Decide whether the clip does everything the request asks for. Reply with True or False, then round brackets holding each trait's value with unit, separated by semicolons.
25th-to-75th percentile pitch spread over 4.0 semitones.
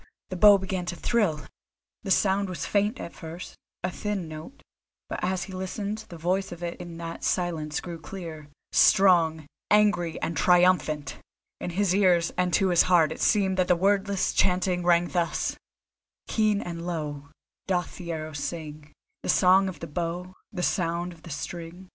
False (2.4 semitones)